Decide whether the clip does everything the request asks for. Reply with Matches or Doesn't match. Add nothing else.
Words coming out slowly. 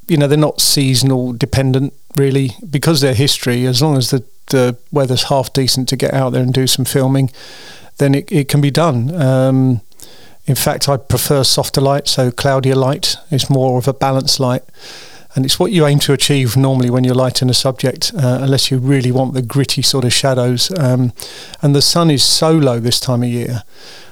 Doesn't match